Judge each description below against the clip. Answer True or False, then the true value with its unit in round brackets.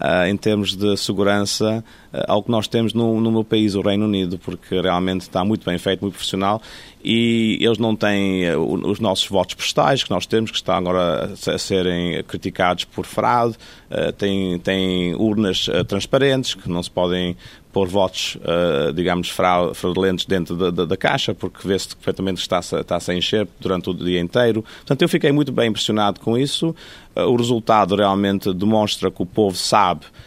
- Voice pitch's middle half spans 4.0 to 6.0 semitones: False (3.3 semitones)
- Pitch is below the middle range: True (100 Hz)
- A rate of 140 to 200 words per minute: True (180 wpm)